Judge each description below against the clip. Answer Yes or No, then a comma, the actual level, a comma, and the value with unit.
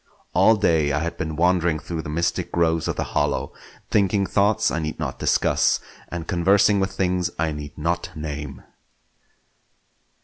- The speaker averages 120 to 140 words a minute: No, average, 160 wpm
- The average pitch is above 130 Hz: No, very low, 85 Hz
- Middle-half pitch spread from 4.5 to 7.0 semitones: No, average, 2.9 semitones